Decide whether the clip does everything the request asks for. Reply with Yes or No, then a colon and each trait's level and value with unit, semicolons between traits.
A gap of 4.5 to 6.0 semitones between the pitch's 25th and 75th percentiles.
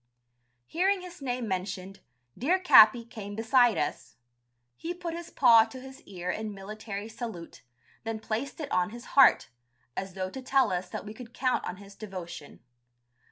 Yes: average, 4.9 semitones